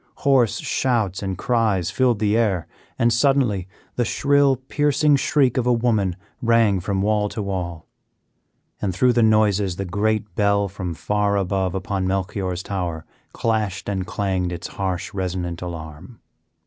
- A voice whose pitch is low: Yes, low, 100 Hz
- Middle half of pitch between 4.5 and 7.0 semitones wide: No, average, 3.8 semitones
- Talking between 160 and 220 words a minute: No, average, 150 wpm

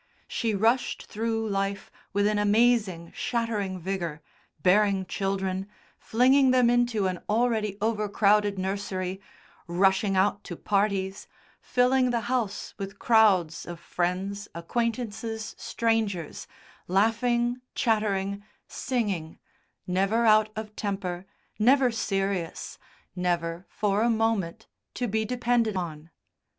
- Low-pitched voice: No, high, 205 Hz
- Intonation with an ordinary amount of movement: Yes, average, 3.1 semitones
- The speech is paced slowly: Yes, slow, 110 wpm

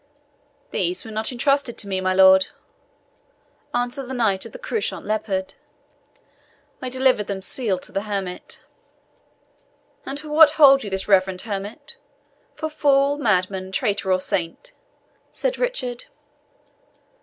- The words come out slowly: Yes, slow, 130 wpm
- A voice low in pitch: No, high, 220 Hz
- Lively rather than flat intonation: Yes, wide, 6.5 semitones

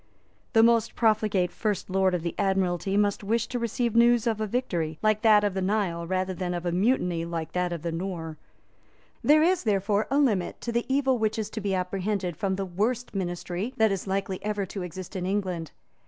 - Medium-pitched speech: No, high, 195 Hz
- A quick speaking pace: Yes, fast, 210 wpm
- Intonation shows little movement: No, average, 3.5 semitones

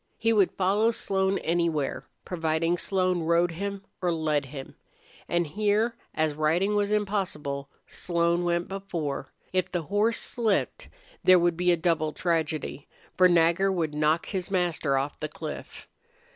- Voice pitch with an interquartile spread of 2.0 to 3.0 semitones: No, average, 3.6 semitones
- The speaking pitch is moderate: Yes, medium, 175 Hz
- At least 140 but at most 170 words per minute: Yes, average, 145 wpm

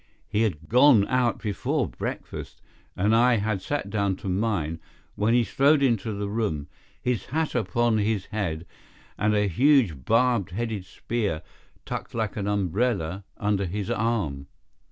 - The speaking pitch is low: Yes, low, 105 Hz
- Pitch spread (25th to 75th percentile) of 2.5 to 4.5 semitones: Yes, average, 3.6 semitones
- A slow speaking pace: No, average, 150 wpm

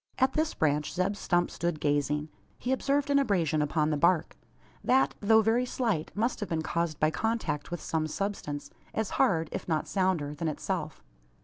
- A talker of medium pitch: Yes, medium, 175 Hz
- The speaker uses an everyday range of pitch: No, wide, 6.3 semitones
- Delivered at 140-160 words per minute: No, average, 180 wpm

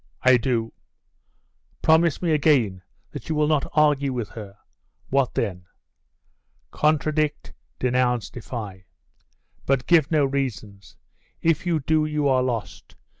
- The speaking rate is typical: No, slow, 125 wpm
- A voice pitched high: No, low, 135 Hz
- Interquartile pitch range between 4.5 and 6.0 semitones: Yes, average, 5.0 semitones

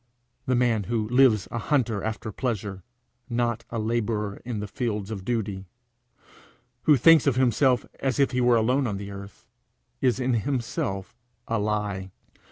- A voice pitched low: Yes, low, 115 Hz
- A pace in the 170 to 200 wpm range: No, average, 160 wpm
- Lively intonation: No, average, 3.2 semitones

